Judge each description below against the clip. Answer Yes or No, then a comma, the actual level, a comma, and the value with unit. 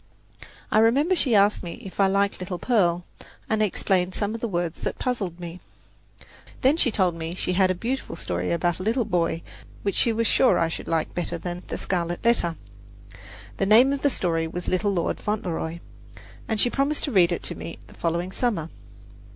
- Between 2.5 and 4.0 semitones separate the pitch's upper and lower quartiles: No, average, 4.7 semitones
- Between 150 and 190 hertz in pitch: Yes, medium, 185 Hz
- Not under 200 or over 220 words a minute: Yes, fast, 205 wpm